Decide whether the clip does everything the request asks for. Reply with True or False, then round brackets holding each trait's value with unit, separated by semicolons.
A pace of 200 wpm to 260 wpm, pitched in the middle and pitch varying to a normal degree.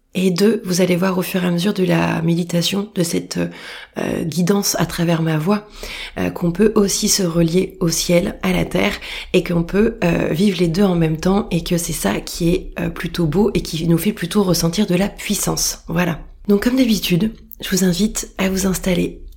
True (215 wpm; 180 Hz; 3.0 semitones)